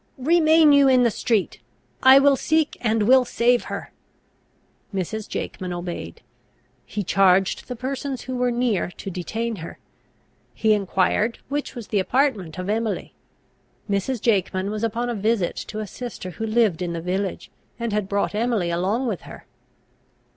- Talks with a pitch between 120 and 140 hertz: No, high, 220 Hz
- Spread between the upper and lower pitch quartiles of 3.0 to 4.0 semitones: No, average, 4.5 semitones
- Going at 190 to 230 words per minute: No, average, 160 wpm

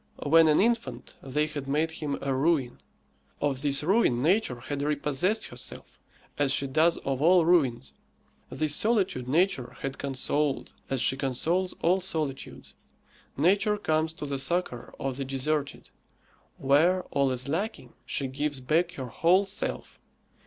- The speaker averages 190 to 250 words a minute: No, average, 145 wpm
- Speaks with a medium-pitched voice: Yes, medium, 150 Hz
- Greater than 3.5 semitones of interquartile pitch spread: Yes, average, 4.2 semitones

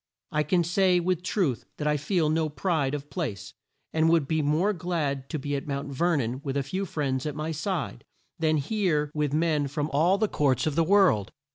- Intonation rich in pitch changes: No, average, 3.5 semitones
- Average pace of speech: No, fast, 215 wpm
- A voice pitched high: No, medium, 155 Hz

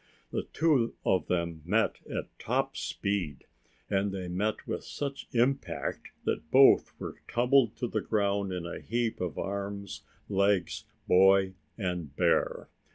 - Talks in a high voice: No, low, 100 Hz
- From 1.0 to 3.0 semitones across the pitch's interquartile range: No, average, 4.1 semitones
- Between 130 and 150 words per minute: Yes, average, 140 wpm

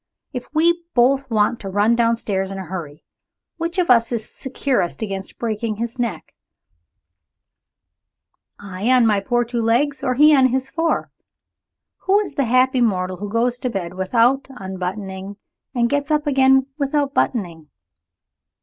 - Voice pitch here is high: Yes, high, 235 Hz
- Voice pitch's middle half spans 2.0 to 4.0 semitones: No, average, 5.2 semitones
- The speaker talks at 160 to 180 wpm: No, average, 150 wpm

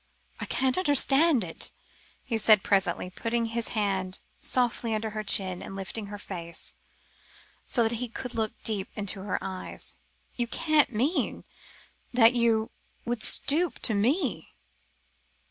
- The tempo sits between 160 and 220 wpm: No, average, 140 wpm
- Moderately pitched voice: No, high, 225 Hz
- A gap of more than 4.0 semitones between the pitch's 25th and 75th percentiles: No, average, 3.7 semitones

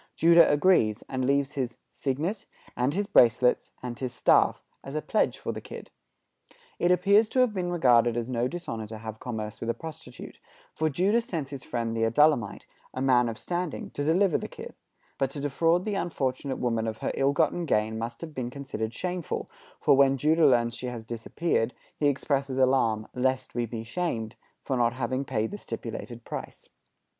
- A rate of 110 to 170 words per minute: No, average, 190 wpm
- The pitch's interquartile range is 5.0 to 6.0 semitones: Yes, wide, 5.4 semitones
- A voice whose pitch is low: Yes, low, 130 Hz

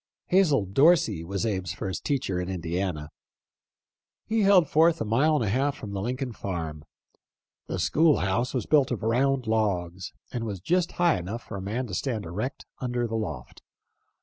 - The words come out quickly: No, average, 175 wpm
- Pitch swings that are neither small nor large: No, wide, 6.4 semitones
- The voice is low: Yes, low, 115 Hz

